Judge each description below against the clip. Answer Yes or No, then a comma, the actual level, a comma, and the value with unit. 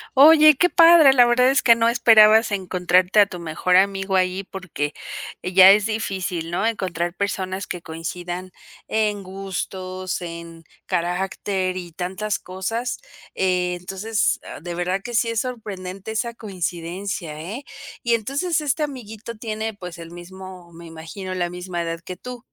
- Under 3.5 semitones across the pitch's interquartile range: No, average, 3.8 semitones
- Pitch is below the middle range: No, high, 190 Hz